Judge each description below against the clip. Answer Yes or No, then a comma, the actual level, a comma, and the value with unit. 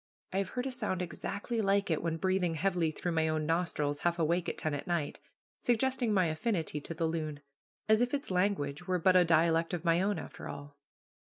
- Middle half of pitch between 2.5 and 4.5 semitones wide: Yes, average, 3.5 semitones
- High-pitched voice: No, medium, 175 Hz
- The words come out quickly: Yes, fast, 215 wpm